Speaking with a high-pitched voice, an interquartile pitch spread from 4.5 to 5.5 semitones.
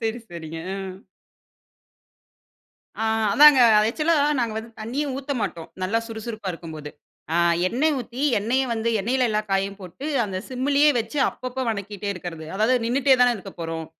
Yes: high, 220 Hz; average, 5.0 semitones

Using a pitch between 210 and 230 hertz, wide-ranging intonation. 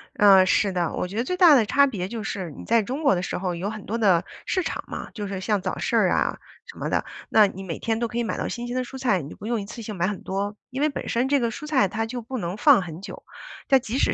No: high, 215 Hz; average, 4.3 semitones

